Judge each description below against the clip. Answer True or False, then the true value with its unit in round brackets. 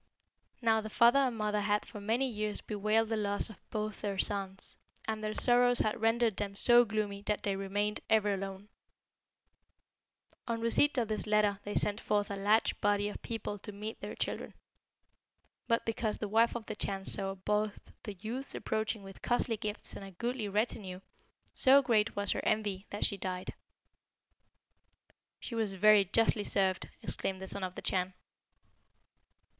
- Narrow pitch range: True (2.0 semitones)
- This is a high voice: True (210 Hz)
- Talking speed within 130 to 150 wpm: False (170 wpm)